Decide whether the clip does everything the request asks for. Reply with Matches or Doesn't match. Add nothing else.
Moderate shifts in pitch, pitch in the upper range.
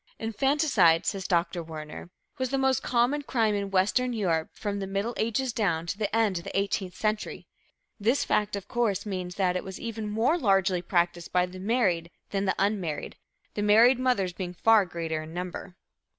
Matches